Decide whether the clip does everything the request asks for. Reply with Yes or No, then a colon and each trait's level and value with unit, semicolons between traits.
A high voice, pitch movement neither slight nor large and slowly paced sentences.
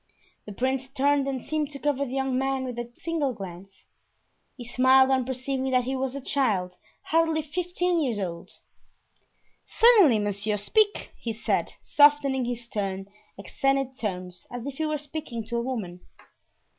No: very high, 260 Hz; average, 4.0 semitones; average, 160 wpm